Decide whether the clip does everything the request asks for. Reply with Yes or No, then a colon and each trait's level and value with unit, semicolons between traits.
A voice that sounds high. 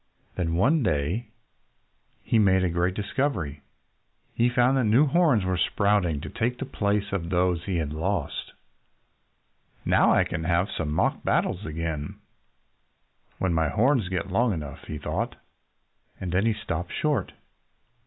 No: very low, 95 Hz